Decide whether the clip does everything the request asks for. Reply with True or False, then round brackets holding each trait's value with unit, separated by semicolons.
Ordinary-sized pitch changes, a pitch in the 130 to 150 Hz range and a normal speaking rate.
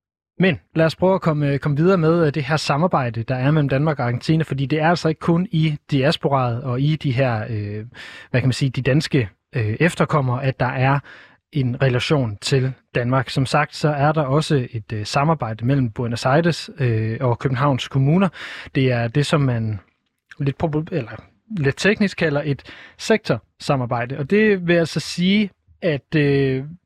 True (4.2 semitones; 140 Hz; 185 wpm)